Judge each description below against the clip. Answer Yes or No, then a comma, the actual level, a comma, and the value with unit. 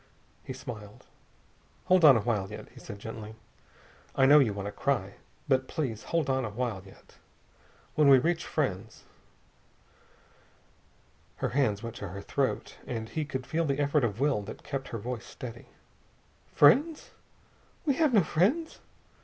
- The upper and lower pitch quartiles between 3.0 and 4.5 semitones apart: No, wide, 5.5 semitones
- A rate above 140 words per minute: Yes, average, 160 wpm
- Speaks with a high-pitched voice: No, low, 130 Hz